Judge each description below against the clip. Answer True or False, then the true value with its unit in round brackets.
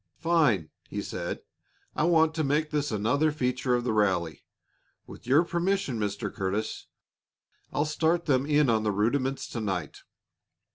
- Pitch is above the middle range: False (130 Hz)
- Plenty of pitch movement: True (6.4 semitones)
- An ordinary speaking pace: True (150 wpm)